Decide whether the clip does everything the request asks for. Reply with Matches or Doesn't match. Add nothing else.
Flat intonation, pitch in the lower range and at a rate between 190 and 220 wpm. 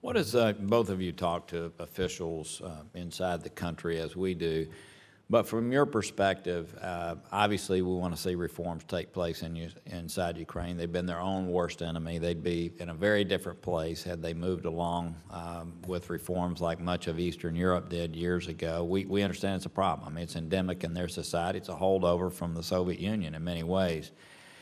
Matches